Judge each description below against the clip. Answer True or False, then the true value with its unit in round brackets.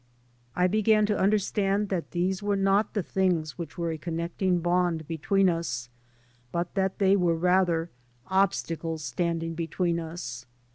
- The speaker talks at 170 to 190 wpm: False (150 wpm)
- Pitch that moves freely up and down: False (2.8 semitones)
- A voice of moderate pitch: True (175 Hz)